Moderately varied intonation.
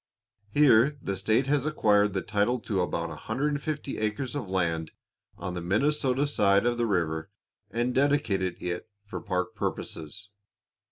No: wide, 6.5 semitones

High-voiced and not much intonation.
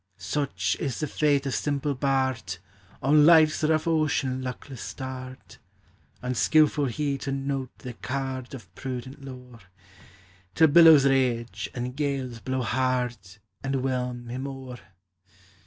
No: low, 130 Hz; narrow, 2.0 semitones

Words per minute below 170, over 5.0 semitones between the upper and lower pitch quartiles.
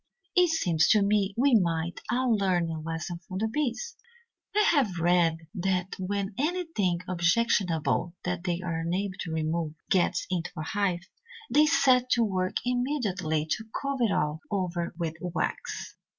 Yes: average, 155 wpm; wide, 5.4 semitones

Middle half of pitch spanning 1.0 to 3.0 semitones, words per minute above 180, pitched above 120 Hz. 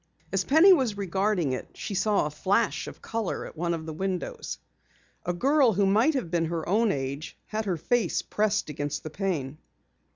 No: average, 5.0 semitones; average, 190 wpm; high, 190 Hz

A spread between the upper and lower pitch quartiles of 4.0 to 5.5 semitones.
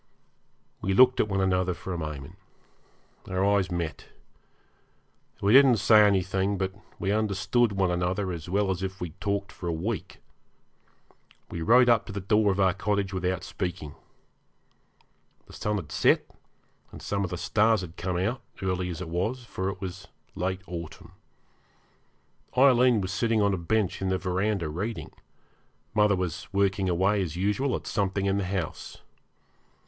No: narrow, 2.4 semitones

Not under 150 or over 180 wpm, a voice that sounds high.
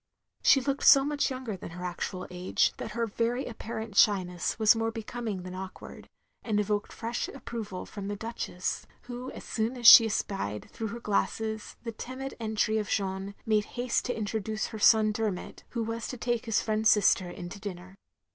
No: average, 190 wpm; high, 220 Hz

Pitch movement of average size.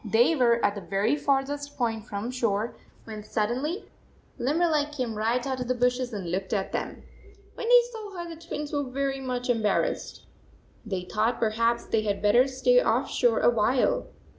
Yes: average, 4.7 semitones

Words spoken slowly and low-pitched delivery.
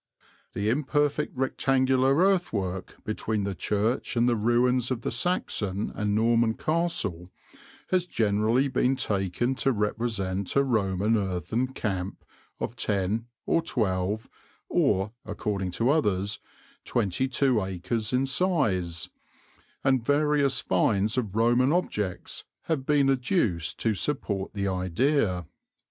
Yes: slow, 120 wpm; low, 115 Hz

